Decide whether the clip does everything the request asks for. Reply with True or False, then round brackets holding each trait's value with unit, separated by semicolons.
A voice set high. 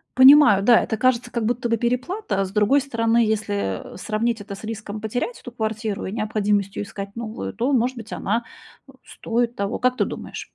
True (225 Hz)